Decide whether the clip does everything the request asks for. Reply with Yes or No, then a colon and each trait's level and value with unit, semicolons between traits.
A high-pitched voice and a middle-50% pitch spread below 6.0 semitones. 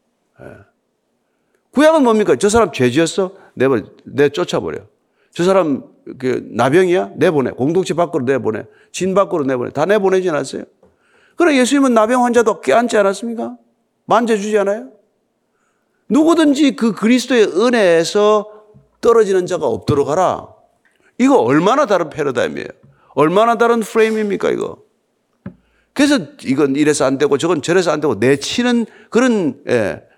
Yes: high, 210 Hz; wide, 5.6 semitones